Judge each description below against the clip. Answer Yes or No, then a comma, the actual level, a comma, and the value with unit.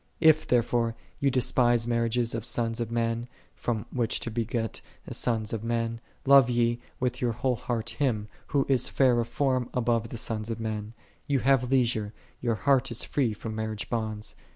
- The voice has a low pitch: Yes, low, 120 Hz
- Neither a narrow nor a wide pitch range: No, narrow, 1.8 semitones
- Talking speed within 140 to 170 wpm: No, average, 180 wpm